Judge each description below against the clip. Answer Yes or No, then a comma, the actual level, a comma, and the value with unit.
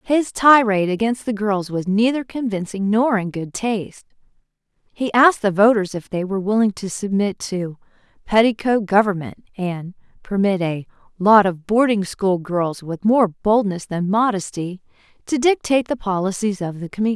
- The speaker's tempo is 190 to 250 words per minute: No, average, 155 wpm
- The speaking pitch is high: Yes, high, 205 Hz